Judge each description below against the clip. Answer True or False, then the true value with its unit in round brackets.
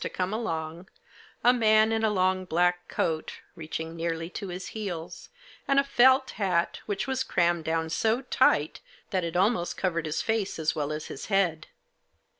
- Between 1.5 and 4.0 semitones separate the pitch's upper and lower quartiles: False (4.9 semitones)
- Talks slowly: False (175 wpm)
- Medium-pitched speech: True (180 Hz)